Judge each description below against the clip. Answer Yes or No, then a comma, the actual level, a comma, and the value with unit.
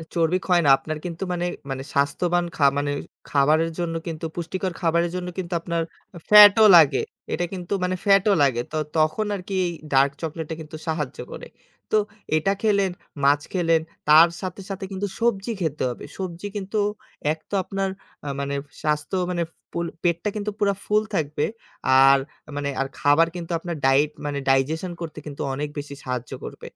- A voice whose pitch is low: No, medium, 170 Hz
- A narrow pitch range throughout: No, average, 4.0 semitones